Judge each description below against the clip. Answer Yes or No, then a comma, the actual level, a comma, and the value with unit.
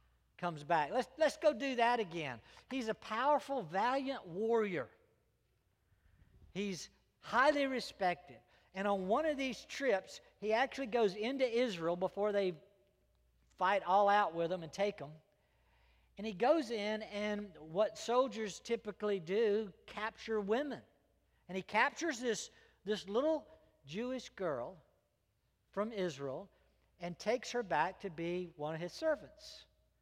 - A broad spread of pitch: Yes, wide, 6.1 semitones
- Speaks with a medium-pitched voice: No, high, 205 Hz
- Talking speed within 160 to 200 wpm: No, slow, 135 wpm